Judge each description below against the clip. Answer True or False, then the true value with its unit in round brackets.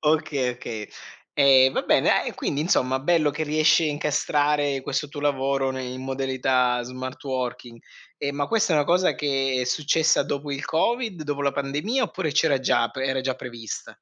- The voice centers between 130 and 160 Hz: True (140 Hz)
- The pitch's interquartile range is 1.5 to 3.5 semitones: True (2.4 semitones)